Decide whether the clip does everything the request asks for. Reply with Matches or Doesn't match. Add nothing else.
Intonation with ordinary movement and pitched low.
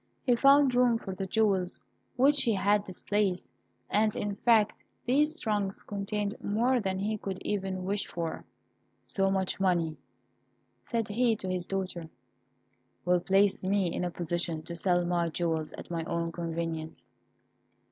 Doesn't match